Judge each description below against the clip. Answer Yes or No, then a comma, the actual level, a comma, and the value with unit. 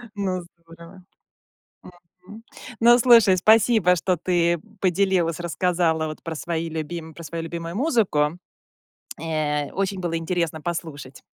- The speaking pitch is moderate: Yes, medium, 170 Hz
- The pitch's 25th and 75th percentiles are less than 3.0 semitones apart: Yes, narrow, 2.6 semitones